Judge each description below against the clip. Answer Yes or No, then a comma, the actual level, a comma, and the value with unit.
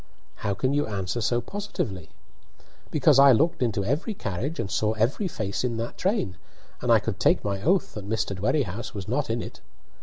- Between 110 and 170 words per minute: No, average, 190 wpm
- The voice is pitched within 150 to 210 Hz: No, low, 115 Hz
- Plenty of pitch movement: Yes, wide, 6.5 semitones